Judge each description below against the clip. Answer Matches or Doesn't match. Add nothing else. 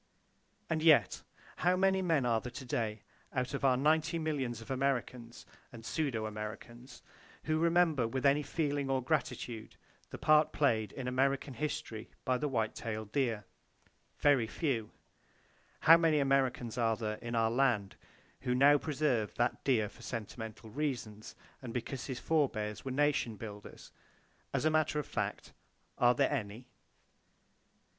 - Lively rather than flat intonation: Doesn't match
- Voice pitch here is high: Doesn't match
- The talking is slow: Doesn't match